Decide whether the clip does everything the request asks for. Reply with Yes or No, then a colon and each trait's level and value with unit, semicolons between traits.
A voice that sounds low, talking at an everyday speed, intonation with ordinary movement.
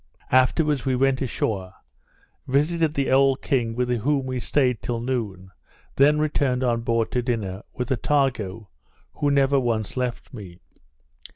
Yes: low, 125 Hz; average, 145 wpm; average, 3.1 semitones